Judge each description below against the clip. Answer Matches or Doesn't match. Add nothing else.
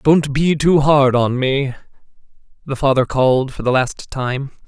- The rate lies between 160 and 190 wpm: Matches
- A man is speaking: Matches